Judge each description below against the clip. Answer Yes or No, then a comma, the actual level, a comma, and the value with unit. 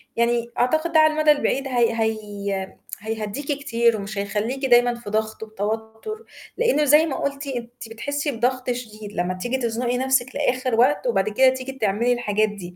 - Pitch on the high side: Yes, high, 240 Hz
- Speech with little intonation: No, average, 3.5 semitones